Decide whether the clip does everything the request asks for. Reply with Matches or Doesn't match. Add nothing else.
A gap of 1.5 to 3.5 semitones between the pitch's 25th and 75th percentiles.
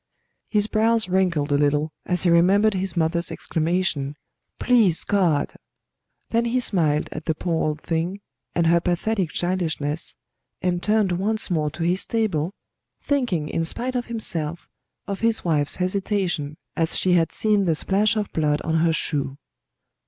Doesn't match